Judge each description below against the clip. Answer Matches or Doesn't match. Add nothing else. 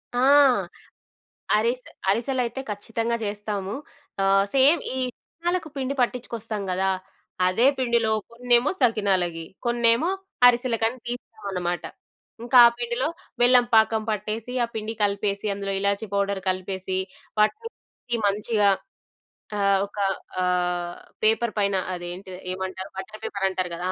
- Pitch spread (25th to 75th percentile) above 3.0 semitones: Matches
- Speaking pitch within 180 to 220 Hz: Matches